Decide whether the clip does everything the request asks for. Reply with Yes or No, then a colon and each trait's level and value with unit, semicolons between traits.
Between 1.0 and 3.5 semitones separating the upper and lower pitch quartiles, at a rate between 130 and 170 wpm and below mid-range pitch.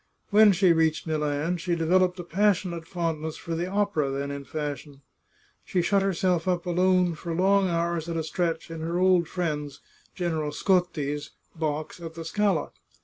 No: average, 2.7 semitones; average, 165 wpm; medium, 170 Hz